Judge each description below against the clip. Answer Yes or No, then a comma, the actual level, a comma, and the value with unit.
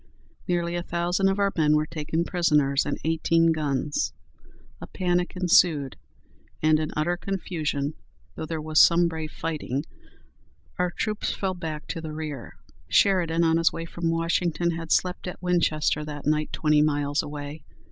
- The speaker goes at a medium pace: Yes, average, 155 wpm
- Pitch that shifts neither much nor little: No, narrow, 2.3 semitones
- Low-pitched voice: No, medium, 160 Hz